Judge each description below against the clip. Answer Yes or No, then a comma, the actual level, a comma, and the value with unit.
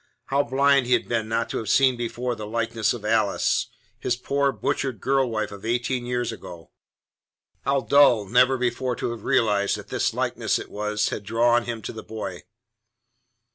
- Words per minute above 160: Yes, average, 180 wpm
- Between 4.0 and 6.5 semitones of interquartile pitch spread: No, average, 2.7 semitones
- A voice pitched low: Yes, low, 120 Hz